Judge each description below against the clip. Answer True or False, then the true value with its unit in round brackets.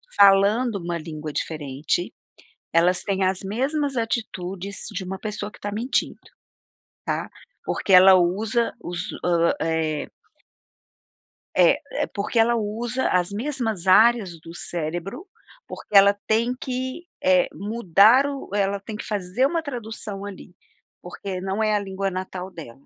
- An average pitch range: True (4.1 semitones)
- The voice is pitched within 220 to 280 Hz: False (200 Hz)